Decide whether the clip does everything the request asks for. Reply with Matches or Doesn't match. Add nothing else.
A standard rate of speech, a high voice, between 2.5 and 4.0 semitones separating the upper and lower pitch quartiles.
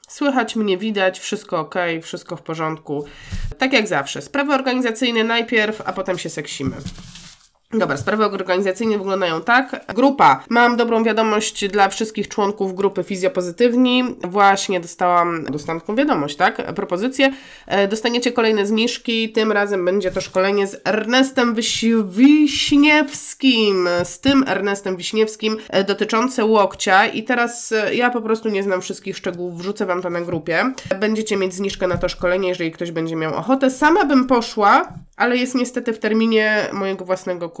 Doesn't match